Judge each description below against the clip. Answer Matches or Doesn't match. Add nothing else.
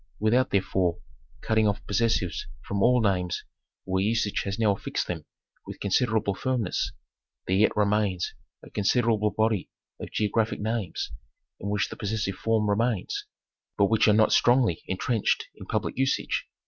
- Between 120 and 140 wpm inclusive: Doesn't match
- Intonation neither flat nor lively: Doesn't match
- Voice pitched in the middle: Doesn't match